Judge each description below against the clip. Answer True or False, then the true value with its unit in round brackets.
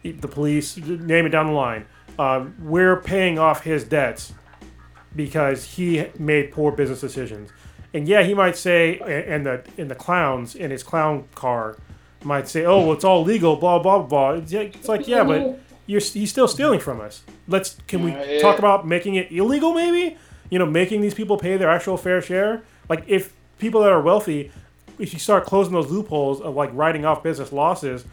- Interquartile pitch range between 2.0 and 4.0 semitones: False (5.1 semitones)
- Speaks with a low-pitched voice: False (165 Hz)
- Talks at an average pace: True (195 wpm)